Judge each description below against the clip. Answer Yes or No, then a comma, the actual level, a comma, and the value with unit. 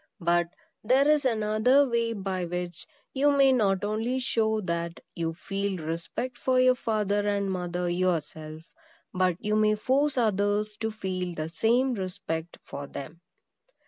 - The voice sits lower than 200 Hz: No, high, 205 Hz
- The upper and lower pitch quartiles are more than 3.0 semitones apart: Yes, average, 4.9 semitones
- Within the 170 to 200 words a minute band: No, average, 145 wpm